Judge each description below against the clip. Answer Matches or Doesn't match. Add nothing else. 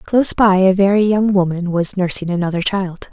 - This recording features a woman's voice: Matches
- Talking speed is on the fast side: Doesn't match